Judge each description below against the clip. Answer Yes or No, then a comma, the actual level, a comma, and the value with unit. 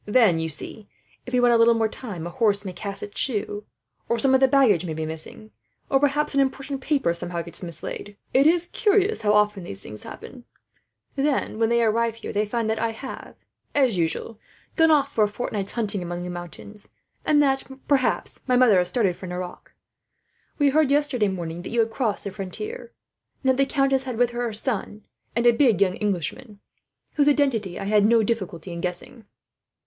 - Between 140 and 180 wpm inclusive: No, fast, 205 wpm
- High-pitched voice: Yes, high, 225 Hz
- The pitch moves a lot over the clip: Yes, wide, 5.7 semitones